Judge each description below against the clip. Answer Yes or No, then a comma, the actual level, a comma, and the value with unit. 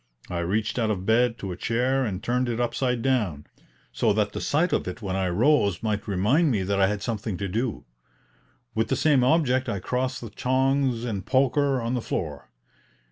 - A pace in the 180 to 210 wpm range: Yes, average, 200 wpm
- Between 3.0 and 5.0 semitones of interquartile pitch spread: Yes, average, 4.5 semitones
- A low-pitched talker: Yes, low, 115 Hz